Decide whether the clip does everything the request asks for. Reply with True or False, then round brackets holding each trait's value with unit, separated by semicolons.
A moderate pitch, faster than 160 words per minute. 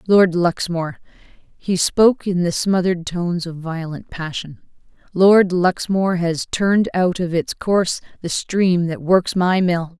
False (180 Hz; 150 wpm)